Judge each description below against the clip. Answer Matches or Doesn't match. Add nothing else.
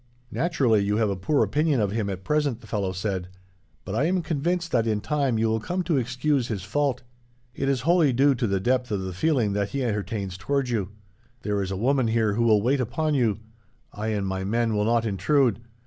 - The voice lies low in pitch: Matches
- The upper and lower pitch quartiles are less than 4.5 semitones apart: Doesn't match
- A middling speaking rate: Doesn't match